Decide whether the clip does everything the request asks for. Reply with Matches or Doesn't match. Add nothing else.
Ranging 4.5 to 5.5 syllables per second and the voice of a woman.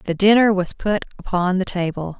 Matches